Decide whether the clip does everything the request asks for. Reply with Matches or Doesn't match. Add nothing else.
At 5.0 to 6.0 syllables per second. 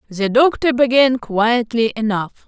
Doesn't match